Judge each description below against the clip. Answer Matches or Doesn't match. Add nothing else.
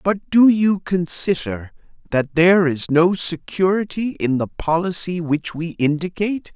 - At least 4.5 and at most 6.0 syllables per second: Doesn't match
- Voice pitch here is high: Doesn't match